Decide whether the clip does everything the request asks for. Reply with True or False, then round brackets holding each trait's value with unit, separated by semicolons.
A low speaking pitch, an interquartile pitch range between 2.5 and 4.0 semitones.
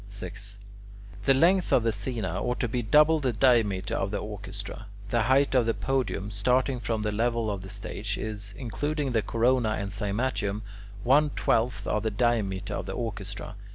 True (110 Hz; 3.7 semitones)